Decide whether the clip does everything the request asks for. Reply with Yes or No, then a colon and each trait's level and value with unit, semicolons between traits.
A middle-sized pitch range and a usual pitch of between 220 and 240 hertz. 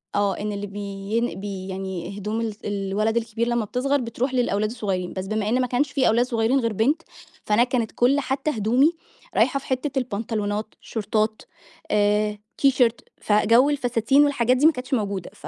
Yes: average, 3.6 semitones; high, 225 Hz